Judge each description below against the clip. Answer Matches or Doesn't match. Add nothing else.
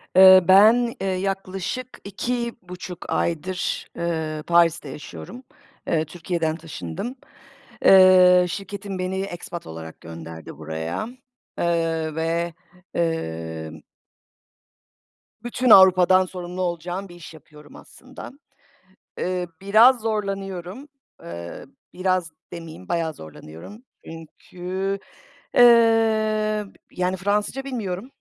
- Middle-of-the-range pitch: Matches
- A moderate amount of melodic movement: Matches